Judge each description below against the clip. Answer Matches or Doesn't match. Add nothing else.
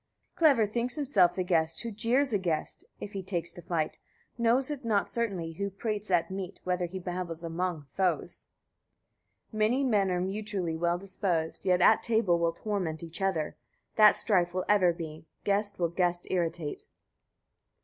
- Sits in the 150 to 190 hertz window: Matches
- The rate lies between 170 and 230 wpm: Matches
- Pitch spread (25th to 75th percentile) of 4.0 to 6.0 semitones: Doesn't match